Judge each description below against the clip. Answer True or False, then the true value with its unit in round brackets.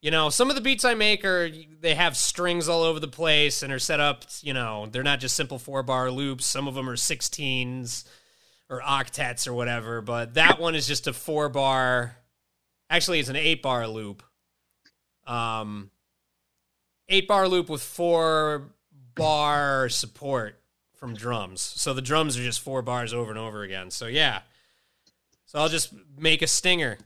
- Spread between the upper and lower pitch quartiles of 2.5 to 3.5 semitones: False (4.7 semitones)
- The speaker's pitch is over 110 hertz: True (135 Hz)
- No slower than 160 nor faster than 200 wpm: True (180 wpm)